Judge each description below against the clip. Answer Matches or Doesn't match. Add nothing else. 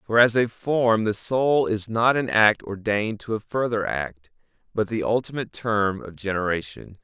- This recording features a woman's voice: Doesn't match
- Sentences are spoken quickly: Doesn't match